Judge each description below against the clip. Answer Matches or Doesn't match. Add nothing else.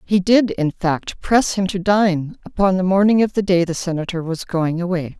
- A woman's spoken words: Matches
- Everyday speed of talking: Doesn't match